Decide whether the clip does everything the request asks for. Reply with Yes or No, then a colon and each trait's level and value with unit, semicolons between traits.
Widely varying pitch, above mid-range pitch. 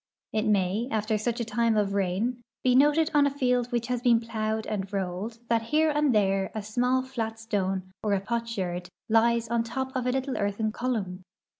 No: average, 3.5 semitones; high, 225 Hz